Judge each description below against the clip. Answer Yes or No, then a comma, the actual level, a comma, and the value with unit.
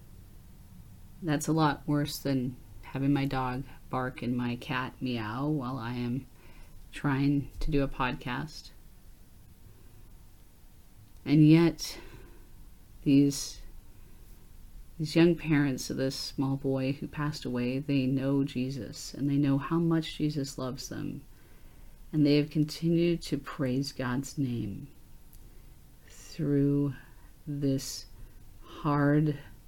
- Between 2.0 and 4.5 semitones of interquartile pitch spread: No, average, 5.1 semitones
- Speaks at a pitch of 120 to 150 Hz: Yes, low, 135 Hz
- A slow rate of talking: Yes, slow, 115 wpm